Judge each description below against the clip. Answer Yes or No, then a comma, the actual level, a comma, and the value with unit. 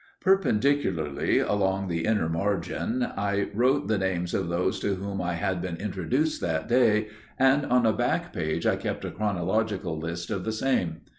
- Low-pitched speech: Yes, low, 100 Hz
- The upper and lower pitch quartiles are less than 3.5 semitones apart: No, average, 4.3 semitones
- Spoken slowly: No, average, 170 wpm